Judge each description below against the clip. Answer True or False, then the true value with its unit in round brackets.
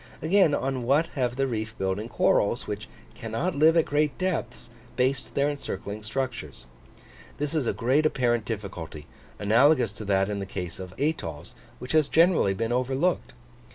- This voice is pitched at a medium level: False (125 Hz)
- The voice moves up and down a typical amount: False (5.9 semitones)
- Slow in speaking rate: False (160 wpm)